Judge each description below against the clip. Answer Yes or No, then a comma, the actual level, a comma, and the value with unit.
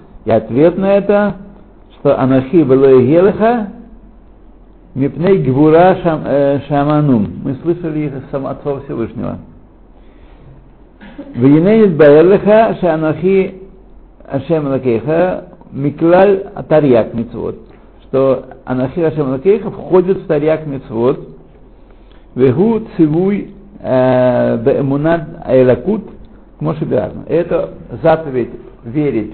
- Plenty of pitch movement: Yes, wide, 6.0 semitones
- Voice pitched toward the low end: No, medium, 155 Hz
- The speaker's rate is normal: No, slow, 85 wpm